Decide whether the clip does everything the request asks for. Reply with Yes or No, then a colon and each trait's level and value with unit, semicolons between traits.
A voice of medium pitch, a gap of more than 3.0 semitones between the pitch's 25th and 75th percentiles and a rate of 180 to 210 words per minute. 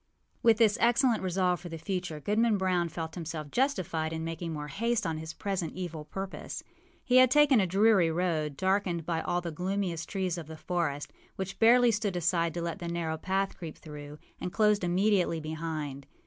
Yes: medium, 175 Hz; average, 3.7 semitones; average, 190 wpm